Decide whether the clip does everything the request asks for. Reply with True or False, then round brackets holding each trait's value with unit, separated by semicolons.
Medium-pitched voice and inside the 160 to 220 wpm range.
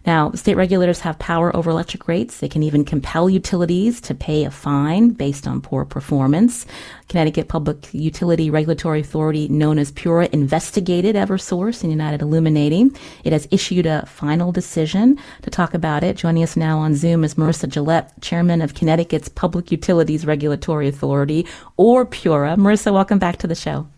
True (165 Hz; 170 wpm)